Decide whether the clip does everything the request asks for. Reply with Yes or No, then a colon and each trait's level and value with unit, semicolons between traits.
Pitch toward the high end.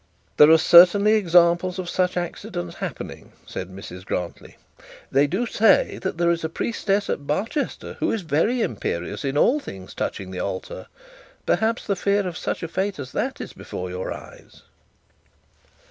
No: medium, 170 Hz